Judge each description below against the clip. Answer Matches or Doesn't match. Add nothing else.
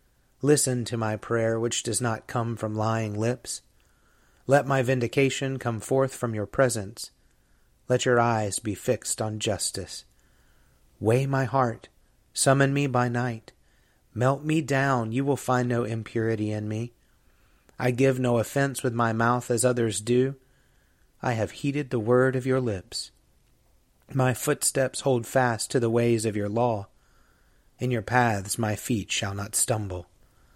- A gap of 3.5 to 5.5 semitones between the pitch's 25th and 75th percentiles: Doesn't match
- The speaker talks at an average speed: Matches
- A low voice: Matches